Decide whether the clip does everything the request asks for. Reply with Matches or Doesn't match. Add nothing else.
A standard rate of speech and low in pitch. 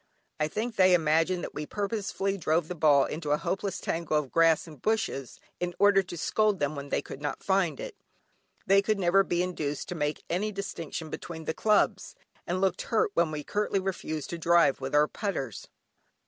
Doesn't match